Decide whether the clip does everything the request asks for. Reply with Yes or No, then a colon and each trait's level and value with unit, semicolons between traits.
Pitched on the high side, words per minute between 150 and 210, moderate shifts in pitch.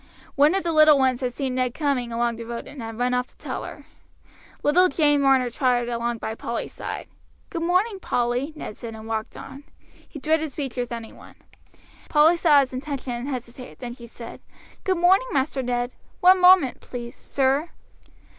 Yes: very high, 260 Hz; average, 190 wpm; average, 4.1 semitones